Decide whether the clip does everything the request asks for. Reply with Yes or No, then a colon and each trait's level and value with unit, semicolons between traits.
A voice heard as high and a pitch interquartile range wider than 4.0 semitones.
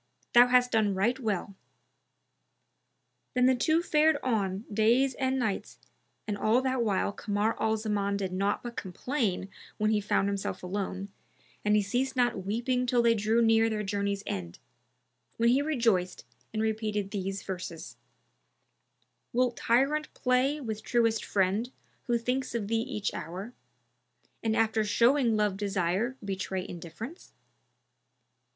No: high, 220 Hz; average, 3.7 semitones